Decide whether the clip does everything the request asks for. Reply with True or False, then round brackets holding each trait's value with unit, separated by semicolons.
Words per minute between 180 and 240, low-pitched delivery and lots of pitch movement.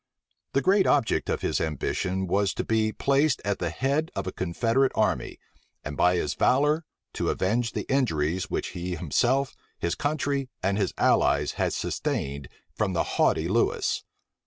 False (160 wpm; 100 Hz; 7.6 semitones)